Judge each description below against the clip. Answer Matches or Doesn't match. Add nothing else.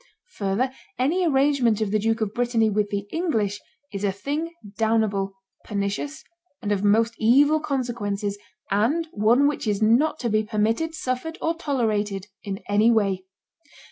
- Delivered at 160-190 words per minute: Doesn't match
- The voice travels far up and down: Doesn't match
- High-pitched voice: Matches